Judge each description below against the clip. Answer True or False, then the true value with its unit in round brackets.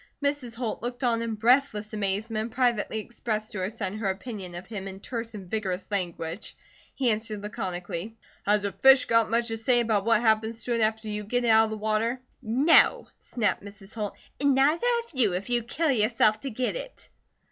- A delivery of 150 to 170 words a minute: False (205 wpm)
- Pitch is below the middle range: False (220 Hz)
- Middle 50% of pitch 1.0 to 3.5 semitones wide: True (2.7 semitones)